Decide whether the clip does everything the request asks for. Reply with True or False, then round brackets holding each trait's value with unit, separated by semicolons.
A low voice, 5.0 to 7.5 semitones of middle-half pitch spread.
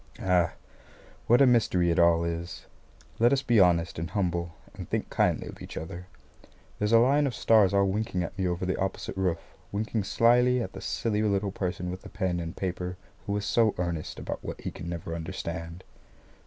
False (95 Hz; 4.1 semitones)